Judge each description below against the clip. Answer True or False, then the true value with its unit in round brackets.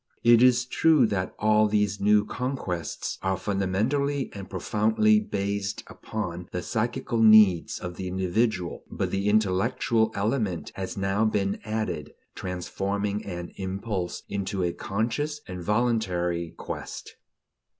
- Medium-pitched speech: False (100 Hz)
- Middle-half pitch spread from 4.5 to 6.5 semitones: False (3.2 semitones)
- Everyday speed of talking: False (125 wpm)